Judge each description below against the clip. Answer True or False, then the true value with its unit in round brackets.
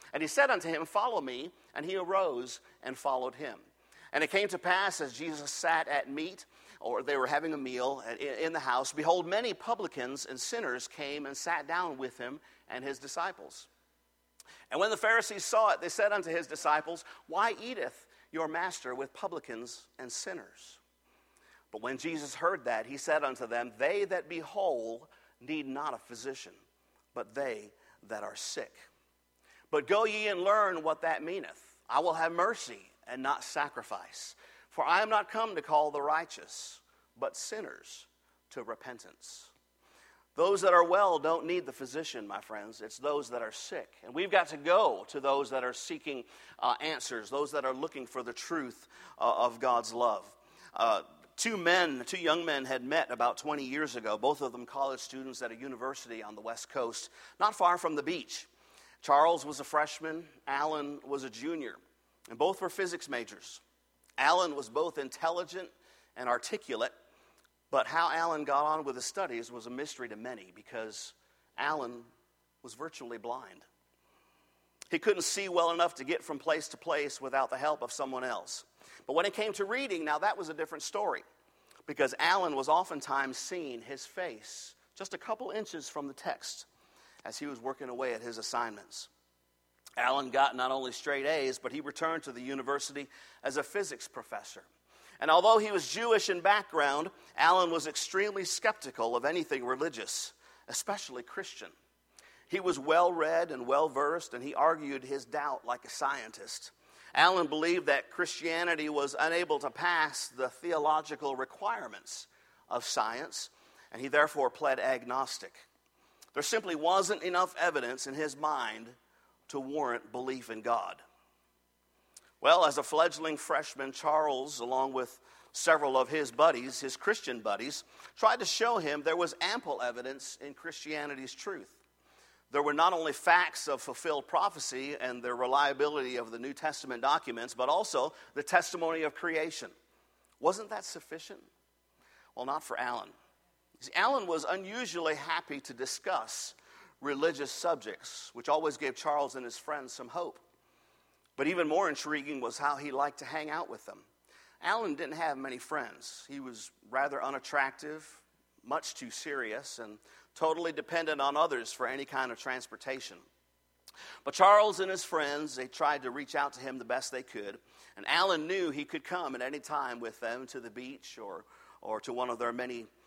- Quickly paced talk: False (170 wpm)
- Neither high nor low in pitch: True (150 Hz)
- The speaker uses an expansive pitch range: False (4.8 semitones)